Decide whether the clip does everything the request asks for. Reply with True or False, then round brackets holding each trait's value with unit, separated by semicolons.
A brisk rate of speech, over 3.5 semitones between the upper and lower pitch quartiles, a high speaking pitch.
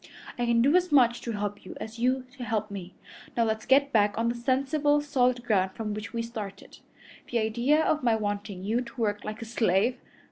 False (215 wpm; 3.2 semitones; 230 Hz)